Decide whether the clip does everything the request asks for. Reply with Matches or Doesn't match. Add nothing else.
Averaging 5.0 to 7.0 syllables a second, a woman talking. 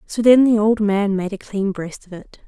Doesn't match